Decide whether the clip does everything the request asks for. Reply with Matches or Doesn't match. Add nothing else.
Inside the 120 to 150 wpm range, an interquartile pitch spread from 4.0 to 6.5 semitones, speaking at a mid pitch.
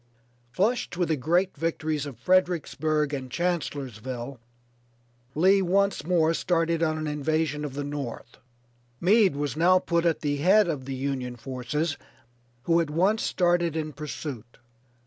Doesn't match